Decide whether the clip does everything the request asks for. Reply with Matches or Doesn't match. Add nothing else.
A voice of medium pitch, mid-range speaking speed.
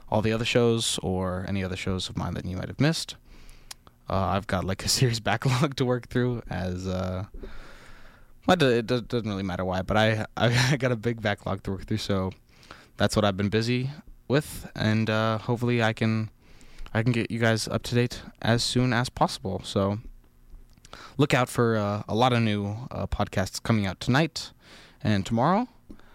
Doesn't match